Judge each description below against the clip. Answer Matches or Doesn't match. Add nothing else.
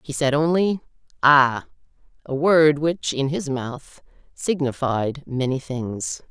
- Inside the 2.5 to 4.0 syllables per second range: Matches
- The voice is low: Doesn't match